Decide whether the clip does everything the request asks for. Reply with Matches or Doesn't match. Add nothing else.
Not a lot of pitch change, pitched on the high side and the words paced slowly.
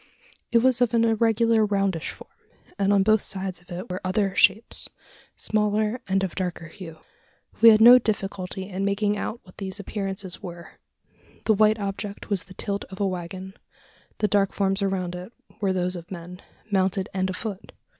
Doesn't match